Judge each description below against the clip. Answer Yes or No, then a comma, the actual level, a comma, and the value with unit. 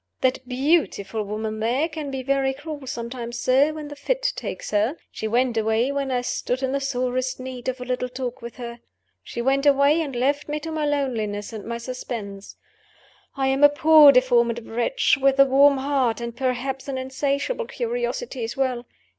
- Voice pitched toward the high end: Yes, very high, 260 Hz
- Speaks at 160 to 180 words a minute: No, average, 190 wpm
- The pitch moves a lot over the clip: No, average, 2.9 semitones